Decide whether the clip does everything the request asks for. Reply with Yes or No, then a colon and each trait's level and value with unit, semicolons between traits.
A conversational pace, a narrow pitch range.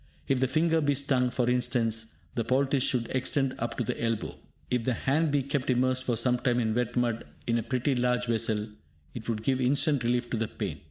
No: fast, 215 wpm; narrow, 2.3 semitones